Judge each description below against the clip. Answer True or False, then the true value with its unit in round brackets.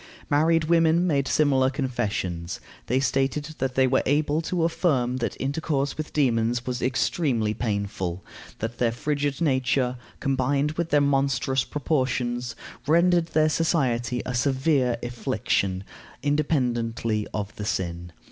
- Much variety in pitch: False (3.7 semitones)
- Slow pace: True (130 wpm)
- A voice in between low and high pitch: False (130 Hz)